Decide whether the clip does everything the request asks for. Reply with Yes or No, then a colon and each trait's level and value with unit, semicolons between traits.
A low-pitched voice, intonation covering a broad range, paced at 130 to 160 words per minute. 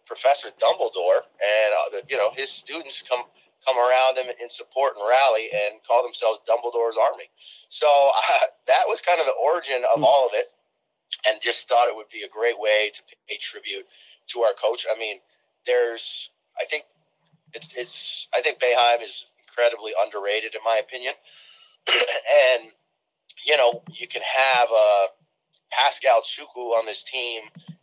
No: low, 125 Hz; wide, 6.6 semitones; average, 170 wpm